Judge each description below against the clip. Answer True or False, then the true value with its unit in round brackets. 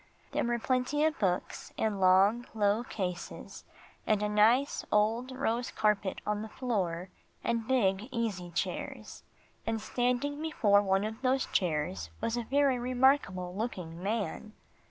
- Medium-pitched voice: False (220 Hz)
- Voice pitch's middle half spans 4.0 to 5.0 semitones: True (4.3 semitones)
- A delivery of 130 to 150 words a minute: True (140 wpm)